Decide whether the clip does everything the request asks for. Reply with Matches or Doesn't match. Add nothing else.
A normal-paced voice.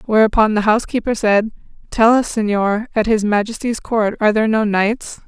Matches